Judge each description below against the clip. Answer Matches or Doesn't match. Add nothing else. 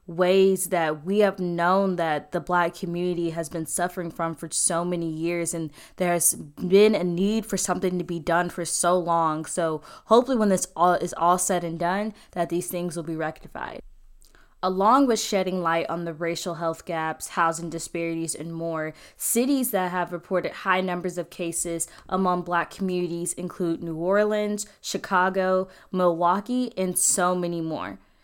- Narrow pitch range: Matches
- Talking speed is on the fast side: Doesn't match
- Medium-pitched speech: Matches